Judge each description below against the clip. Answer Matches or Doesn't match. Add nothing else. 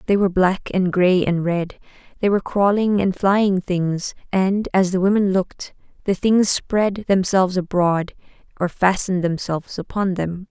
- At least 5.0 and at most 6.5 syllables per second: Doesn't match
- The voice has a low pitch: Doesn't match